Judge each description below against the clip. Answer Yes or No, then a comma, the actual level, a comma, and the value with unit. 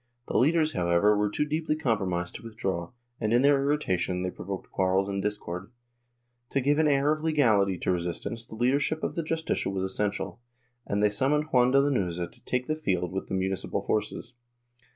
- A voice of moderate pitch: No, low, 105 Hz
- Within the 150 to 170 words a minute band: No, average, 195 wpm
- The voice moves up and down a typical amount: No, wide, 7.1 semitones